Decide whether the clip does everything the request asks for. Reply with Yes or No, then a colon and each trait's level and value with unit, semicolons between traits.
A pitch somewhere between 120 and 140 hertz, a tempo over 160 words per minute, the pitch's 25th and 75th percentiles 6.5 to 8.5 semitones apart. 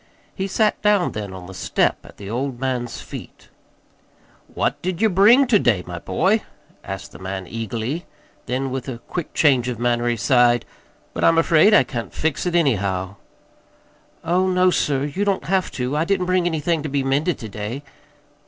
Yes: low, 135 Hz; average, 185 wpm; wide, 7.3 semitones